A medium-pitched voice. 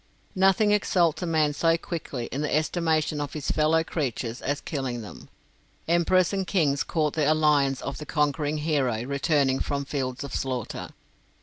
Yes: medium, 150 Hz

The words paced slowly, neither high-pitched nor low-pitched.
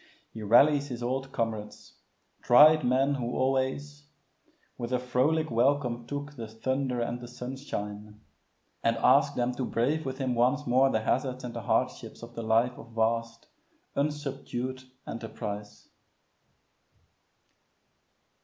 No: slow, 130 wpm; low, 125 Hz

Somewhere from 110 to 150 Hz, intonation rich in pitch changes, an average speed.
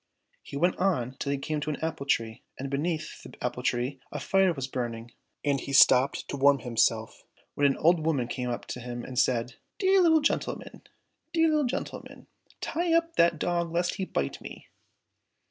Yes: medium, 140 Hz; wide, 5.9 semitones; average, 195 wpm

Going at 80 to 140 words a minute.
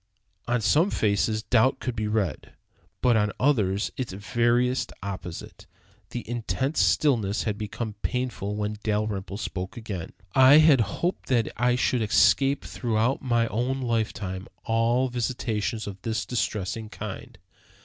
Yes: slow, 135 wpm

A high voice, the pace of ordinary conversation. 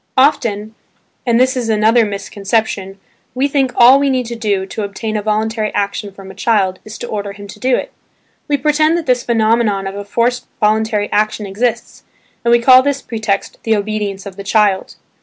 Yes: high, 220 Hz; average, 195 wpm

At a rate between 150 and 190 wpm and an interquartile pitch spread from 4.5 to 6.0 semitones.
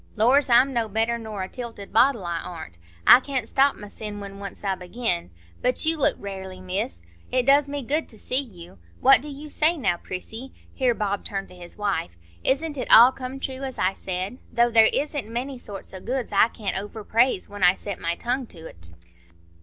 No: average, 200 wpm; wide, 5.5 semitones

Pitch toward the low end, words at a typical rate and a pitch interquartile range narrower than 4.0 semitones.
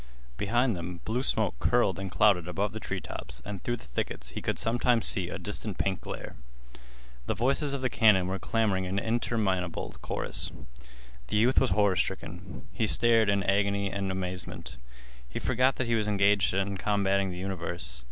Yes: low, 100 Hz; average, 170 wpm; average, 3.2 semitones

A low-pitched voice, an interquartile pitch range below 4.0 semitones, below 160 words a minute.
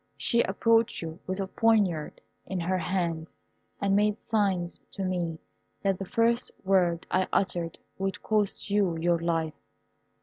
No: medium, 185 Hz; average, 3.1 semitones; average, 145 wpm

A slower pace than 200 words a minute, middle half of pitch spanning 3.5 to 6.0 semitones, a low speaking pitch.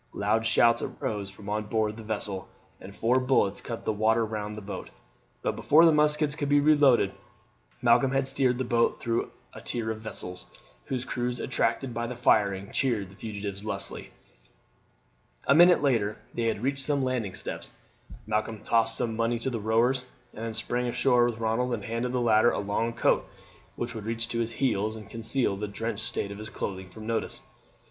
No: average, 190 wpm; average, 2.7 semitones; low, 115 Hz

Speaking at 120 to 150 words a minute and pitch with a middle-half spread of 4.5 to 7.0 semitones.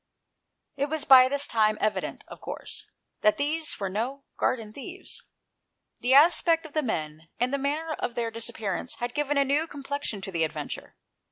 No: average, 175 wpm; average, 5.1 semitones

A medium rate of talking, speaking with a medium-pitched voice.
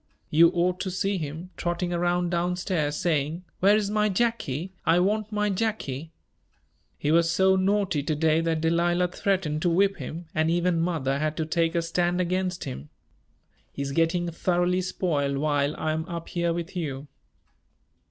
Yes: average, 170 wpm; medium, 170 Hz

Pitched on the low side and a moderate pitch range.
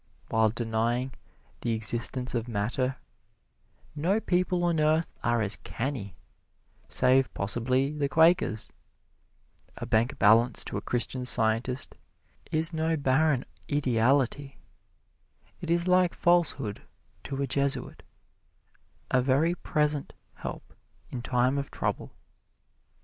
Yes: low, 130 Hz; average, 4.5 semitones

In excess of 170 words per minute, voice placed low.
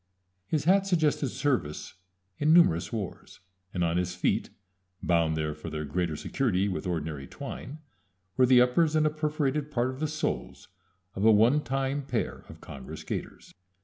No: average, 165 wpm; low, 125 Hz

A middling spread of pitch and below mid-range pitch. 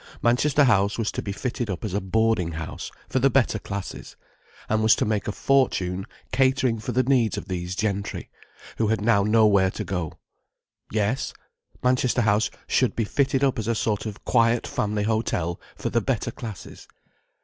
Yes: average, 3.4 semitones; low, 110 Hz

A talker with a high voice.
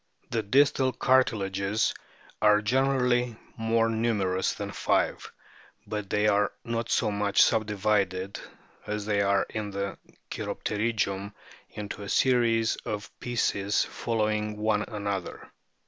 No: low, 105 Hz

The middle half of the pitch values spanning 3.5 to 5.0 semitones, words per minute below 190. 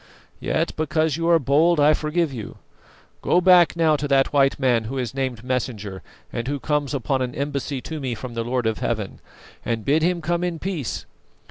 No: average, 4.2 semitones; average, 200 wpm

